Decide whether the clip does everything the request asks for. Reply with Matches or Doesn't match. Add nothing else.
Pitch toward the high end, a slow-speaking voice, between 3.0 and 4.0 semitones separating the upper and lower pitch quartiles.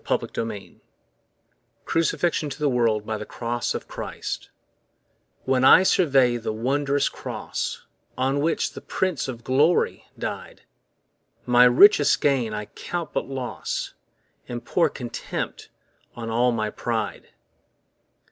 Doesn't match